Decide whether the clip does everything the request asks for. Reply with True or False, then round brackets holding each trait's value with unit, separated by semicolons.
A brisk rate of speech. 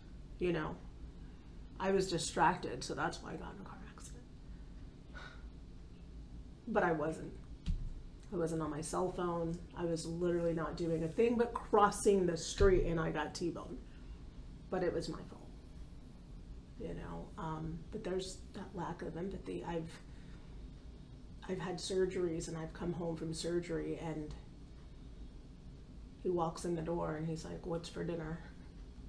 False (155 wpm)